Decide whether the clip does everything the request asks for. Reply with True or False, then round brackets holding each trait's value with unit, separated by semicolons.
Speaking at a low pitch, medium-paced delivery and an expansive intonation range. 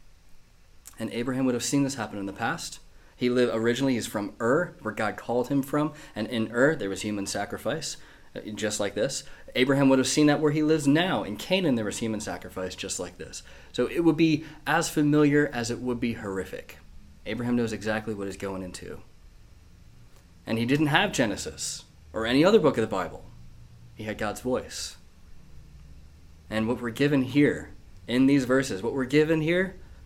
True (120 Hz; 190 wpm; 7.0 semitones)